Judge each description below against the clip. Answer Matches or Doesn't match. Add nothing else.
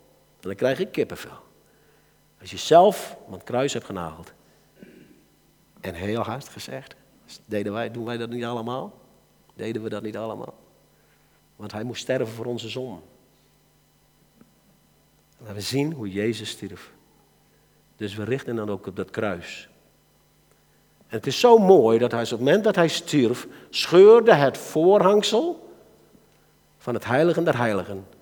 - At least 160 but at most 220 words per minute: Doesn't match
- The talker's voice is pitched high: Doesn't match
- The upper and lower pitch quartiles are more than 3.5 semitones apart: Matches